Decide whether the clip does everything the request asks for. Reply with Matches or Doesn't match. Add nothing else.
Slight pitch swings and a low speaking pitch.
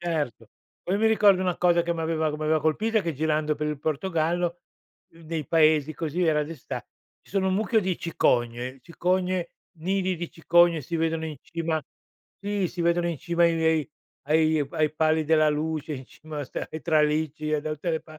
Doesn't match